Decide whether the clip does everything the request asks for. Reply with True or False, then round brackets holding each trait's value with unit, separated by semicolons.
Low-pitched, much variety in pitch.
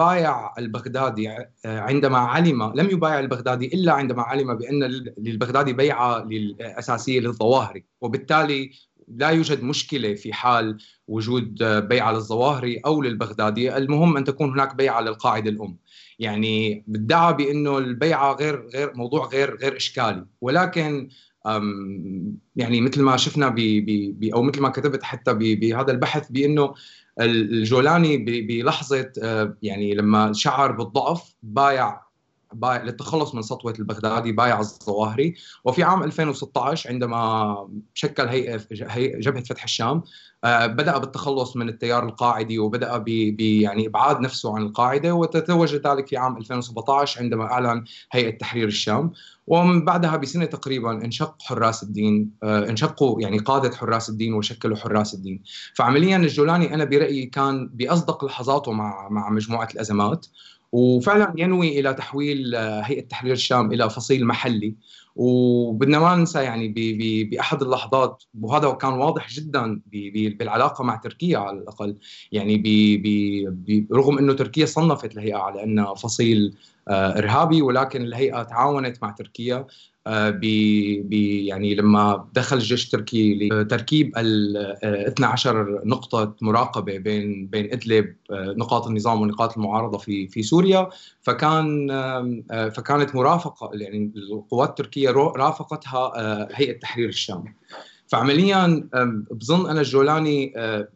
False (120 Hz; 4.3 semitones)